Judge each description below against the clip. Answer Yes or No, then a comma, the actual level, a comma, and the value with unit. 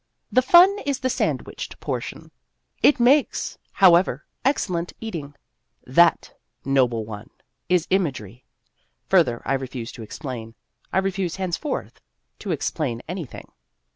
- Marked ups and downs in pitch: Yes, wide, 7.7 semitones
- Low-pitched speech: No, medium, 170 Hz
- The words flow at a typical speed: No, slow, 115 wpm